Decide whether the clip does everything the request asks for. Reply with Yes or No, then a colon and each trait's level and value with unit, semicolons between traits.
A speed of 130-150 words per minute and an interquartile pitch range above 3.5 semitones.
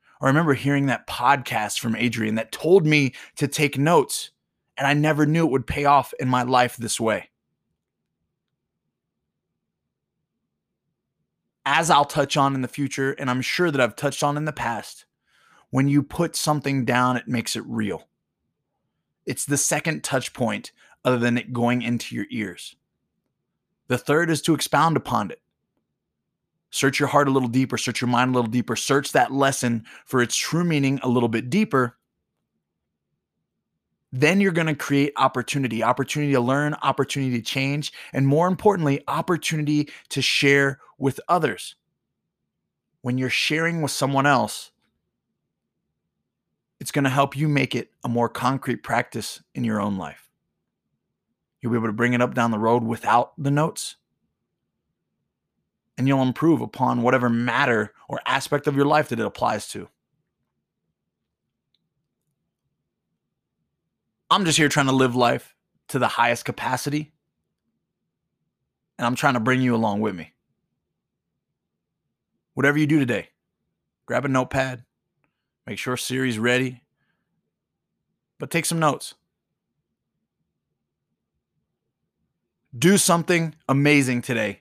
No: average, 145 wpm; average, 3.1 semitones